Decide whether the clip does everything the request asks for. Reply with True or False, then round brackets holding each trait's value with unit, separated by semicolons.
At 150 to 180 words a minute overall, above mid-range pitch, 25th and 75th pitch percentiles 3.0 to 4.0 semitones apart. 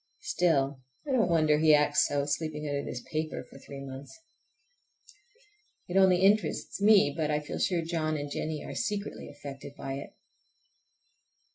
False (155 wpm; 155 Hz; 3.7 semitones)